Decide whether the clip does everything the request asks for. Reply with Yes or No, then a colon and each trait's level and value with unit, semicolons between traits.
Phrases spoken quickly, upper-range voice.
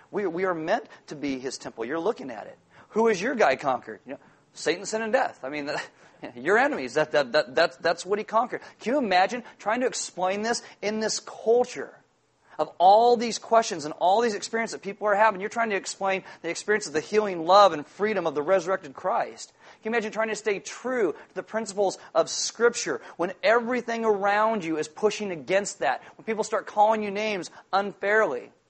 Yes: fast, 210 wpm; high, 210 Hz